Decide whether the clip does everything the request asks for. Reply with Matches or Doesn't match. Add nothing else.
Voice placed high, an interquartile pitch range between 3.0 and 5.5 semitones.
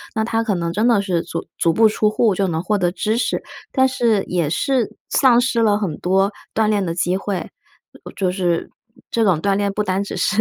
Matches